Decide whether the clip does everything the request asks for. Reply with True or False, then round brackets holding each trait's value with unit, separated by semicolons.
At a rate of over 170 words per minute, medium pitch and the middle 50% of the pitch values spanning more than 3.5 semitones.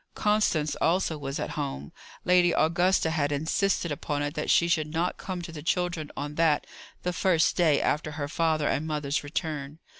False (180 wpm; 160 Hz; 2.9 semitones)